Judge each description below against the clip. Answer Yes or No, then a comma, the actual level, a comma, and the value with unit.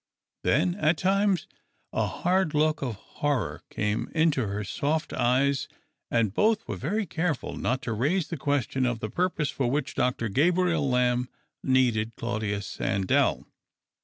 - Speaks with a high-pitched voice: No, medium, 140 Hz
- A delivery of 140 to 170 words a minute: Yes, average, 145 wpm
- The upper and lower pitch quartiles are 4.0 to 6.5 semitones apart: Yes, wide, 5.6 semitones